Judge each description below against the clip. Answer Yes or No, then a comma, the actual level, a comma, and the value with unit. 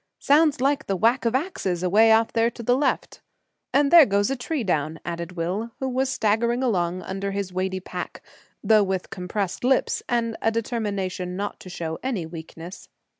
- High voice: Yes, high, 215 Hz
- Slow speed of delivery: No, average, 180 wpm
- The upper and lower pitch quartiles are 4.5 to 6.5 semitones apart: Yes, average, 5.1 semitones